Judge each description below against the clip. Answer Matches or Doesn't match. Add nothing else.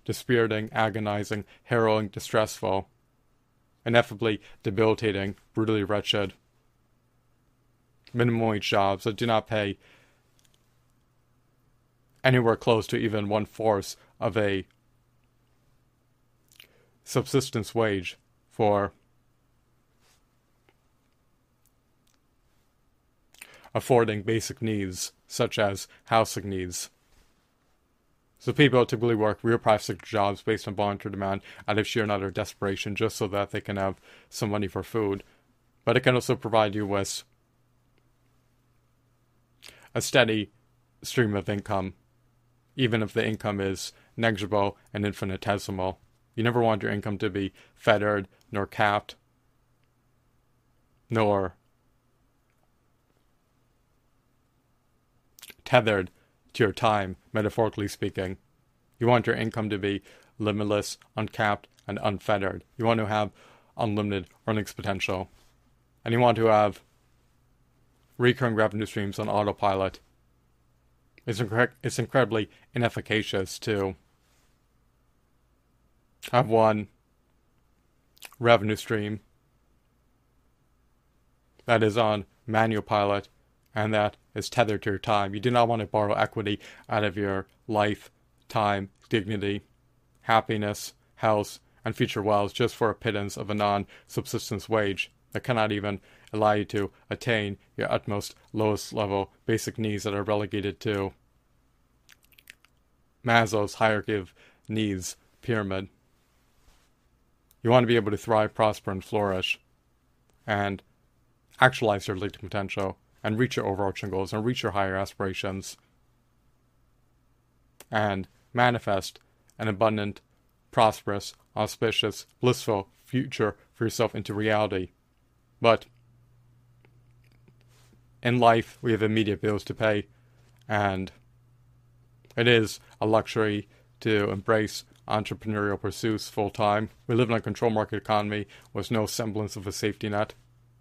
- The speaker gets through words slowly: Matches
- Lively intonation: Doesn't match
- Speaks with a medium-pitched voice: Doesn't match